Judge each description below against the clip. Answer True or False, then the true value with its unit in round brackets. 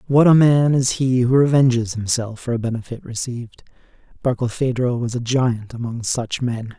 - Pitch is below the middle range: True (125 Hz)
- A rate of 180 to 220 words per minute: False (170 wpm)